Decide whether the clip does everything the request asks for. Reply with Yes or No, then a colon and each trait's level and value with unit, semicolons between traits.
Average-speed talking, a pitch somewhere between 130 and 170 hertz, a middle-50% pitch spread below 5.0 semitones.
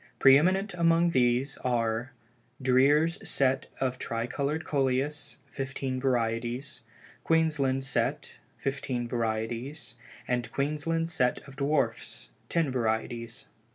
No: slow, 105 wpm; low, 135 Hz; average, 3.5 semitones